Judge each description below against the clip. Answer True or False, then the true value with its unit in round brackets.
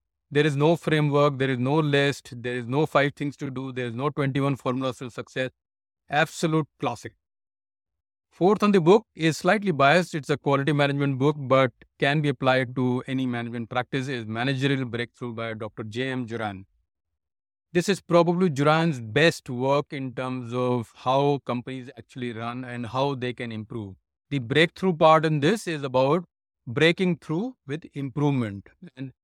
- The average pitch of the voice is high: False (135 Hz)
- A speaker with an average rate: True (170 wpm)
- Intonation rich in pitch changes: False (4.0 semitones)